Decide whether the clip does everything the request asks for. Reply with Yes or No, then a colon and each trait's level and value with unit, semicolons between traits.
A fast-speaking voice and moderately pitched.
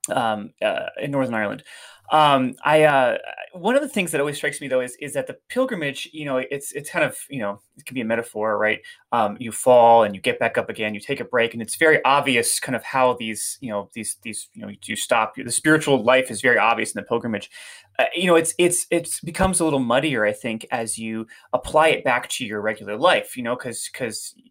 No: fast, 240 wpm; low, 130 Hz